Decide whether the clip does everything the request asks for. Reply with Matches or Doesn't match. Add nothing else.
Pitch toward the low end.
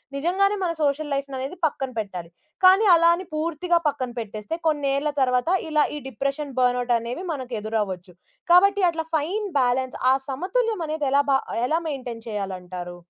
Doesn't match